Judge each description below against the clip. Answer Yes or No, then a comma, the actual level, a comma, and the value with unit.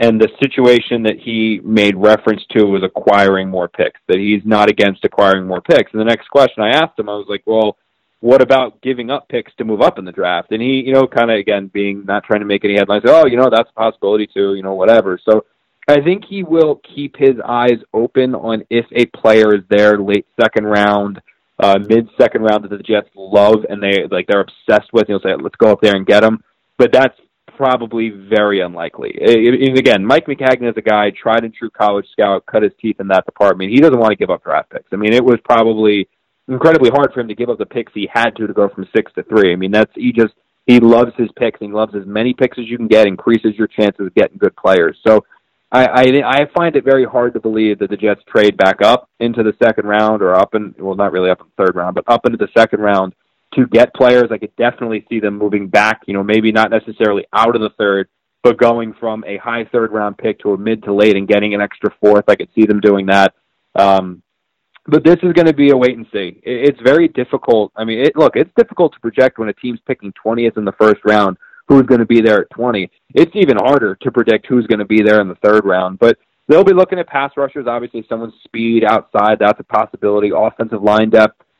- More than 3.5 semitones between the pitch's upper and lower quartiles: No, average, 2.9 semitones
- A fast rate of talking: Yes, fast, 250 wpm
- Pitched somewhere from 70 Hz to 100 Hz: No, low, 110 Hz